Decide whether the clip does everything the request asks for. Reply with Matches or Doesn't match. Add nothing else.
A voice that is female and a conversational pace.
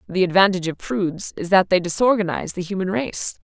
Matches